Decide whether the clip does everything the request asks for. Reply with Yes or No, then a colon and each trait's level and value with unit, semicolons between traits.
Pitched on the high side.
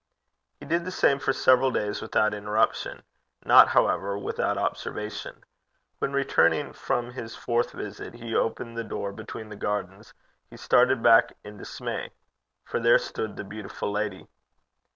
No: low, 110 Hz